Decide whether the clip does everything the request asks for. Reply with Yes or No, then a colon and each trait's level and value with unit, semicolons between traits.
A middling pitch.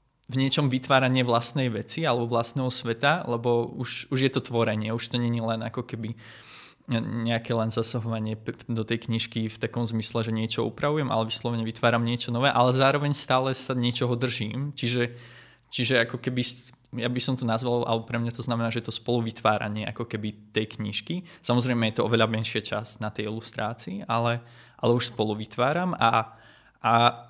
No: low, 120 Hz